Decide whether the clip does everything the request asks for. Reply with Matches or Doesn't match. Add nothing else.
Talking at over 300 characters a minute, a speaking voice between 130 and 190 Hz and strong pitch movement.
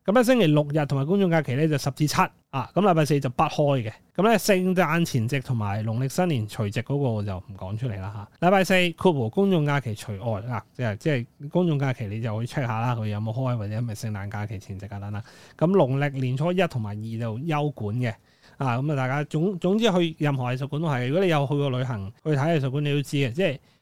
Matches